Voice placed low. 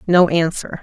No: medium, 170 Hz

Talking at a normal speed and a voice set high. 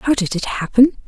No: fast, 225 wpm; high, 230 Hz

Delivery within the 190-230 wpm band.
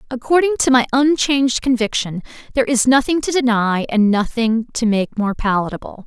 No: average, 160 wpm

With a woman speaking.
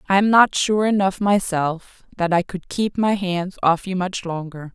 Yes: female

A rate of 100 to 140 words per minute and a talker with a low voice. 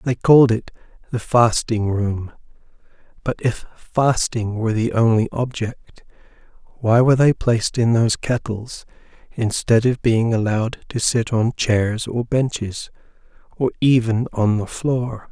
Yes: slow, 135 wpm; low, 115 Hz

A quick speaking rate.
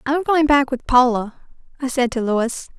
No: average, 195 wpm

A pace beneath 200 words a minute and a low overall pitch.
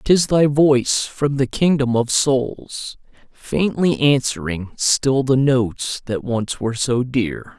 Yes: average, 140 wpm; low, 130 Hz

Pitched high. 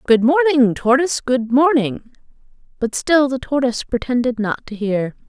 Yes: very high, 250 Hz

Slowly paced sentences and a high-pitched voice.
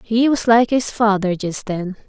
No: average, 200 wpm; high, 215 Hz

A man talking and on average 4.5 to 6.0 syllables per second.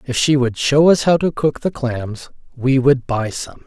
No: male; 4.2 syllables/s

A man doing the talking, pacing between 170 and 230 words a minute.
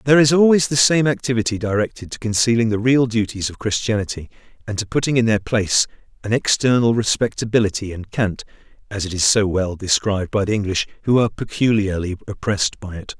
Yes: male; average, 180 wpm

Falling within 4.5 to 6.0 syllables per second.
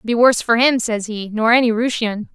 Yes: 5.5 syllables/s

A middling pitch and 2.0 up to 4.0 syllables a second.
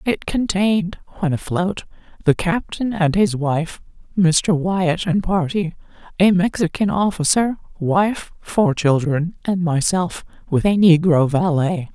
Yes: medium, 175 Hz; 3.9 syllables/s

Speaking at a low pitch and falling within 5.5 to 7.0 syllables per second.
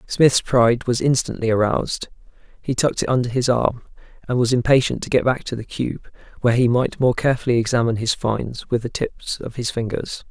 Yes: low, 120 Hz; 5.8 syllables/s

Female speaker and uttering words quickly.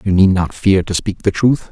No: male; fast, 280 wpm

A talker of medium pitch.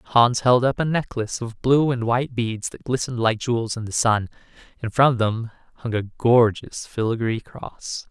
No: low, 120 Hz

